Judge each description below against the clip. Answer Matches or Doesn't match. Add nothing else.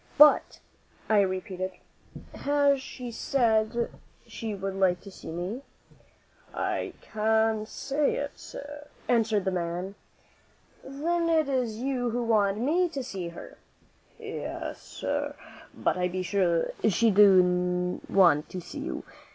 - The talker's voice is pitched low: Doesn't match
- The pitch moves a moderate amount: Doesn't match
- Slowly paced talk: Matches